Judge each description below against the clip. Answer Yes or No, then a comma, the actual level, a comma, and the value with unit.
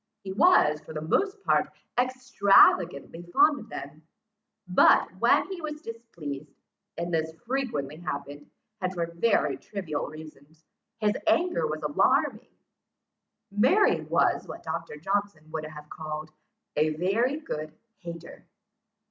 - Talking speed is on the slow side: Yes, slow, 125 wpm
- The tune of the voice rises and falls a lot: Yes, wide, 6.9 semitones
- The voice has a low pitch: No, medium, 170 Hz